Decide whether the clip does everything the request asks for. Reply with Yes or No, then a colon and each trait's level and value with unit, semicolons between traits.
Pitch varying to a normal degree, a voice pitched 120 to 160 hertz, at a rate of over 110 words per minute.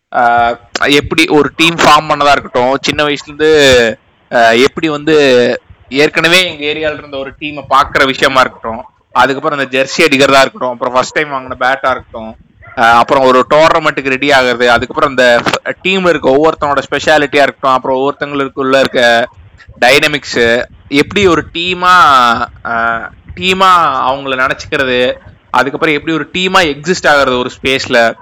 Yes: average, 3.4 semitones; low, 135 Hz; average, 125 wpm